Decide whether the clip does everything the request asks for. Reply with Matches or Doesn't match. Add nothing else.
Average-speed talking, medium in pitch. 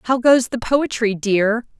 Doesn't match